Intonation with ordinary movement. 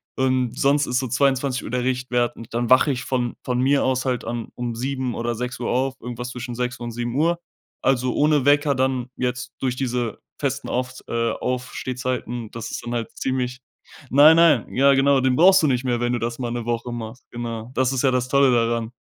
No: narrow, 1.7 semitones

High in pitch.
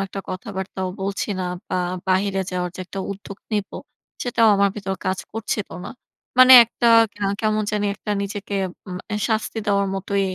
Yes: high, 200 Hz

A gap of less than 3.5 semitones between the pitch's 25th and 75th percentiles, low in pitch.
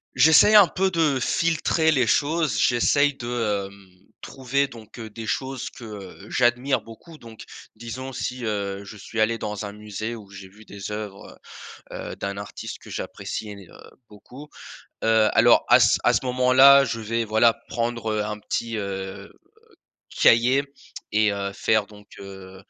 No: average, 3.8 semitones; low, 115 Hz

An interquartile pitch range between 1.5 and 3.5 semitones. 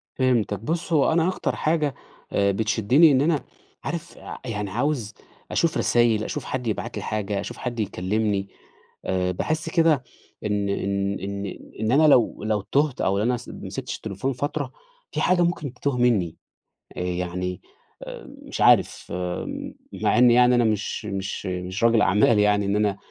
No: wide, 5.4 semitones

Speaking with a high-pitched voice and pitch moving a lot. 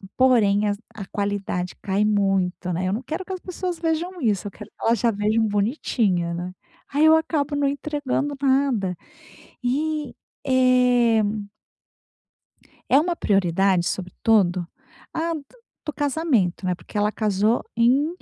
Yes: high, 230 Hz; wide, 6.4 semitones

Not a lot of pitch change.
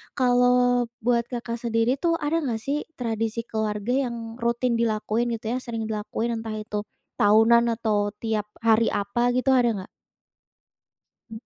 Yes: narrow, 2.0 semitones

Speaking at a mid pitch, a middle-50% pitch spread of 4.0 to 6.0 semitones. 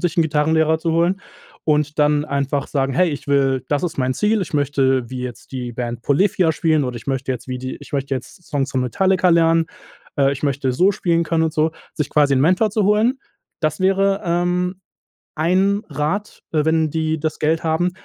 Yes: medium, 155 Hz; average, 4.3 semitones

